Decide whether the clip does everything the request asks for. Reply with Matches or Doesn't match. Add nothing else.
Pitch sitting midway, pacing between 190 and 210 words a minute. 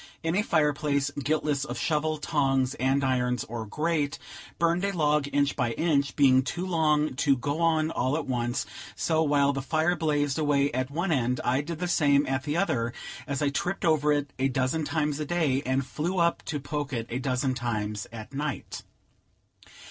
Matches